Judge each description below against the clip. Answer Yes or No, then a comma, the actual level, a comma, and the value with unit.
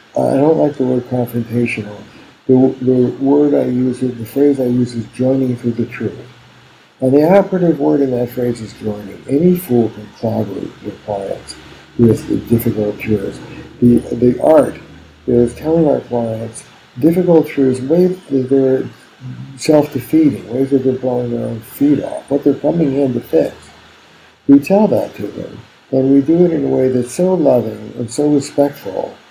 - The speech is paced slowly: No, average, 170 wpm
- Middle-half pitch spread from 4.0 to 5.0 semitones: No, average, 3.3 semitones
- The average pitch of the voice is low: Yes, low, 130 Hz